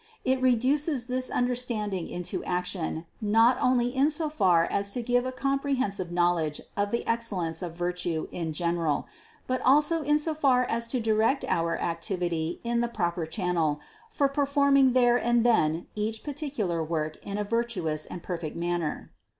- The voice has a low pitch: No, high, 220 Hz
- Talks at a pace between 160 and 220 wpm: Yes, average, 165 wpm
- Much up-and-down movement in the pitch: Yes, wide, 6.8 semitones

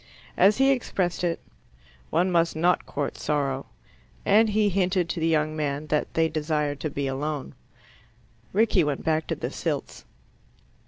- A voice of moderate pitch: Yes, medium, 160 Hz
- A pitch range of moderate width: Yes, average, 3.6 semitones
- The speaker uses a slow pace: No, average, 155 wpm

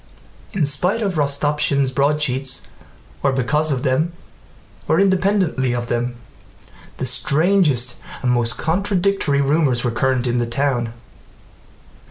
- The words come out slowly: Yes, slow, 120 wpm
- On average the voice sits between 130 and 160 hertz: Yes, medium, 140 Hz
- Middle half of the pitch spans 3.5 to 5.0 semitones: Yes, average, 4.4 semitones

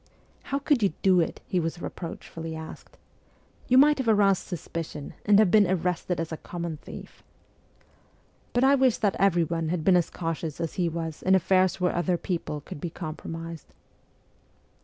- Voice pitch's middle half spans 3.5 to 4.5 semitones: No, average, 3.1 semitones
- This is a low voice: No, medium, 175 Hz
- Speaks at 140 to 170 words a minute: No, average, 185 wpm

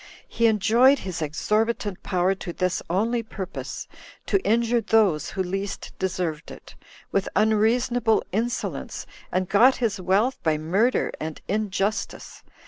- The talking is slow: Yes, slow, 130 wpm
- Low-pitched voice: No, high, 205 Hz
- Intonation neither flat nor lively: Yes, average, 3.7 semitones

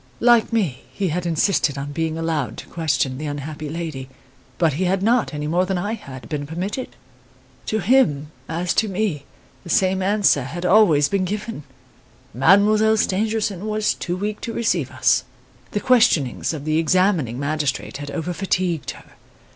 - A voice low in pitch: No, medium, 175 Hz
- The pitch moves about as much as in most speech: No, wide, 5.7 semitones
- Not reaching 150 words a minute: No, average, 165 wpm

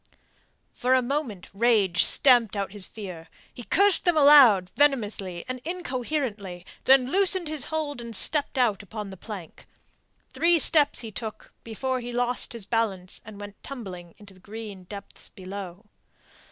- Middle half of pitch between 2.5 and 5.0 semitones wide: No, wide, 5.5 semitones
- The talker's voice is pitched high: Yes, high, 230 Hz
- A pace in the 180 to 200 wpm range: No, average, 155 wpm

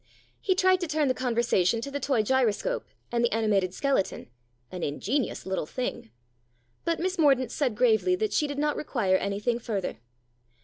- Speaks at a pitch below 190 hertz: No, high, 245 Hz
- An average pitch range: No, wide, 6.2 semitones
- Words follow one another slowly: No, average, 175 wpm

